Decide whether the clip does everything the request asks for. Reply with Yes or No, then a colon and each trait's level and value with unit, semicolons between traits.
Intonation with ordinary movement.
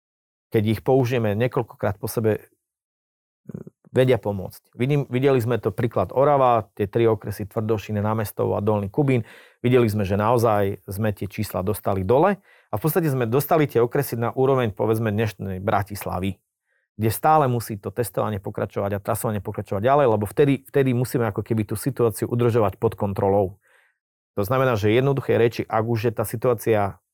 Yes: average, 3.3 semitones